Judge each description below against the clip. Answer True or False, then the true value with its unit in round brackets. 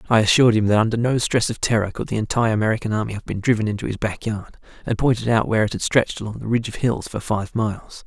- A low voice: True (110 Hz)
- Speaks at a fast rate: True (270 wpm)